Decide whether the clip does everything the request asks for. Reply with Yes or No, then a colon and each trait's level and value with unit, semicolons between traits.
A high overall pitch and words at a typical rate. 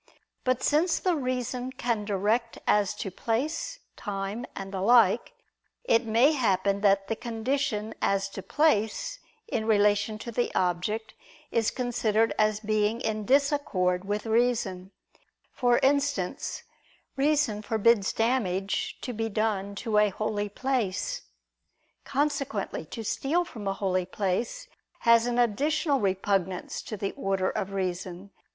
No: high, 220 Hz; slow, 130 wpm